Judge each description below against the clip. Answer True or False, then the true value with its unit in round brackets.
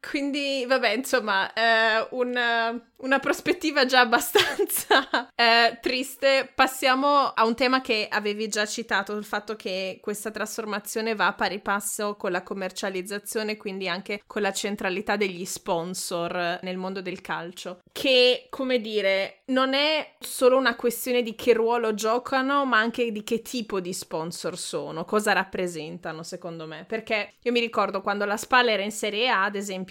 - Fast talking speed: False (160 wpm)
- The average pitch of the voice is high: True (220 Hz)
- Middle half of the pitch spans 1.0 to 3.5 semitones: False (4.3 semitones)